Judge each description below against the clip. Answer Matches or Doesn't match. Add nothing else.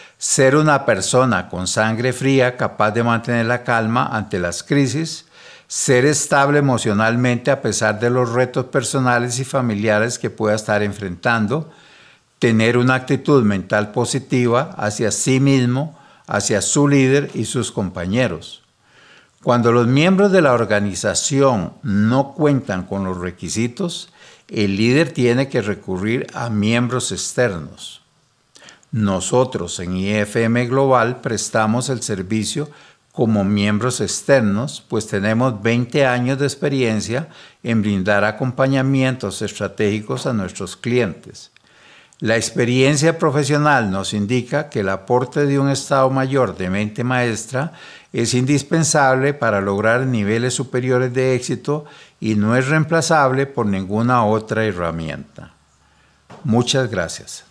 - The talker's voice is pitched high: Doesn't match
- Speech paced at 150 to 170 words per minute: Doesn't match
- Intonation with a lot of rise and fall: Doesn't match